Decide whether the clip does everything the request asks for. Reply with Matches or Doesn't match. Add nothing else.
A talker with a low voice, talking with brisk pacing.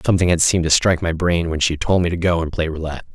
Matches